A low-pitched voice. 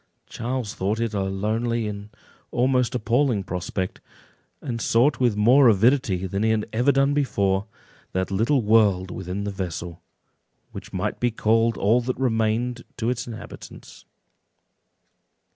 Yes: low, 110 Hz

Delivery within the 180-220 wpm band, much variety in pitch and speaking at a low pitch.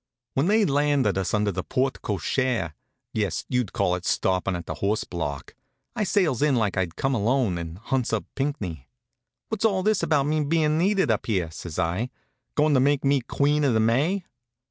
Yes: average, 190 wpm; wide, 7.6 semitones; low, 125 Hz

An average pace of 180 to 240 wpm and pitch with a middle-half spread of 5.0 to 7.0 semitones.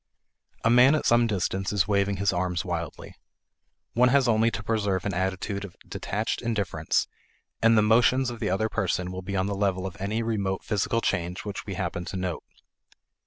No: average, 190 wpm; average, 3.3 semitones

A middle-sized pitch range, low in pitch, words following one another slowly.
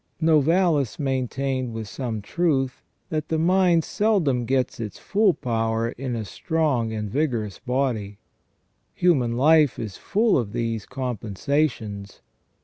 No: wide, 5.7 semitones; low, 130 Hz; slow, 125 wpm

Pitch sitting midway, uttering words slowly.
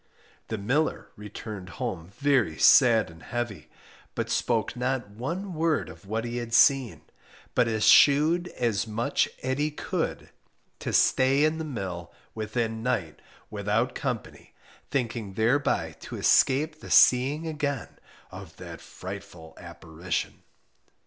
No: low, 120 Hz; slow, 130 wpm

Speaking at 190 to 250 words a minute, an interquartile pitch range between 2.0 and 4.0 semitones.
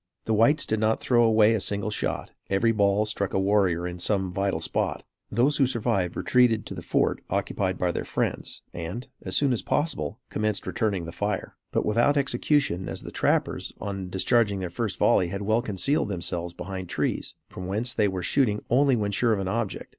Yes: average, 200 wpm; average, 3.7 semitones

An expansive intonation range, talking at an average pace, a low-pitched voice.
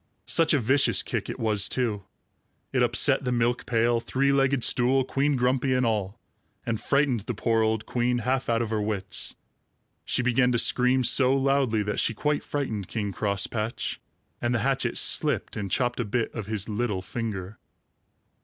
No: average, 3.2 semitones; average, 175 wpm; low, 120 Hz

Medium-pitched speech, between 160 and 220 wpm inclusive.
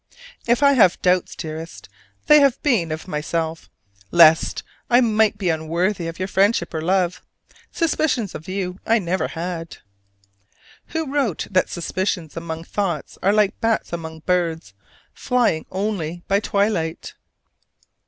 No: medium, 180 Hz; average, 140 wpm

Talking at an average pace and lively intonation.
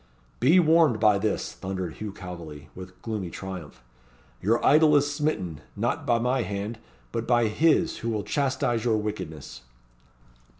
Yes: average, 145 wpm; wide, 5.9 semitones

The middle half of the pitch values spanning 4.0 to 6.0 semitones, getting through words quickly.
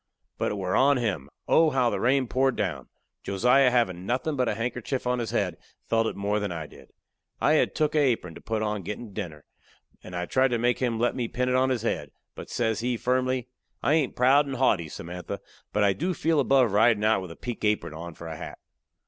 Yes: average, 4.6 semitones; fast, 235 wpm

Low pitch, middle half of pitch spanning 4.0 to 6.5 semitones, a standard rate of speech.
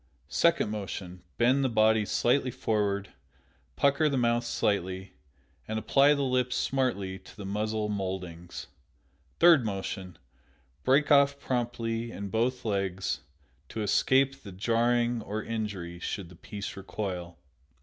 No: low, 110 Hz; average, 4.5 semitones; slow, 130 wpm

